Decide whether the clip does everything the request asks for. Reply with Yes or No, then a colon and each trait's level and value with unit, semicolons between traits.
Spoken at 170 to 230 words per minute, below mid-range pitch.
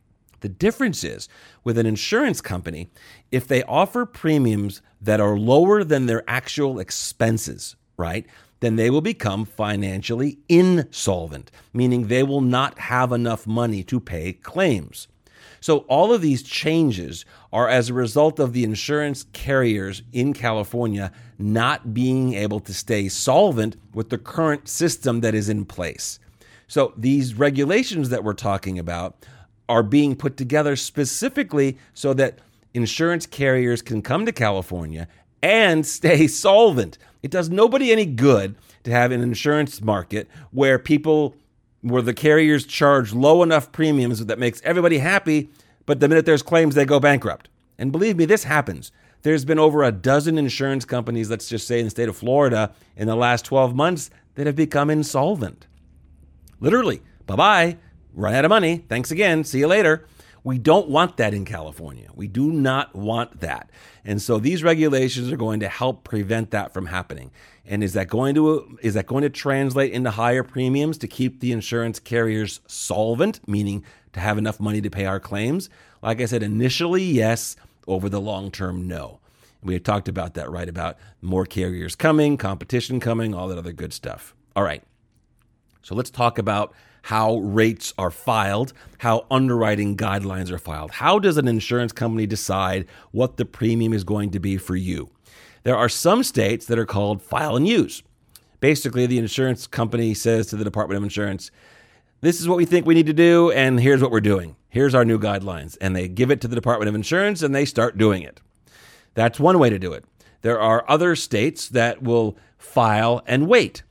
Yes: average, 175 wpm; low, 120 Hz